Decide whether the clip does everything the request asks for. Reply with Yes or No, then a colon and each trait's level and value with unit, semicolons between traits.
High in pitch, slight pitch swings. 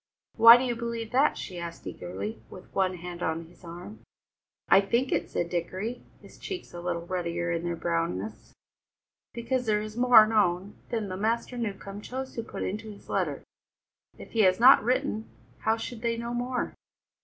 No: high, 210 Hz; average, 5.2 semitones